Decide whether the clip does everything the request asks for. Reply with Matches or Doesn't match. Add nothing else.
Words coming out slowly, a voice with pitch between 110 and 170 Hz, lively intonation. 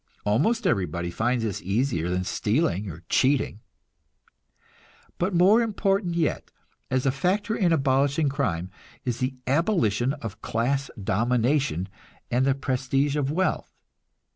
Matches